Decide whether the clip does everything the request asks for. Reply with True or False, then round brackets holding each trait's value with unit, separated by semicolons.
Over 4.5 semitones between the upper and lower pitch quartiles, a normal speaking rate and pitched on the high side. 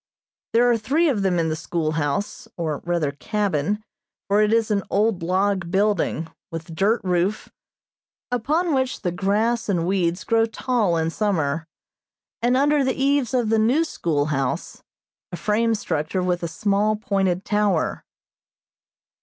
True (5.0 semitones; 145 wpm; 200 Hz)